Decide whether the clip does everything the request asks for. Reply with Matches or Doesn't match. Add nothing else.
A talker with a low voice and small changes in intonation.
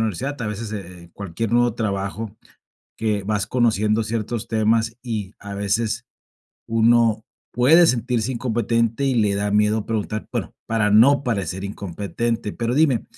Matches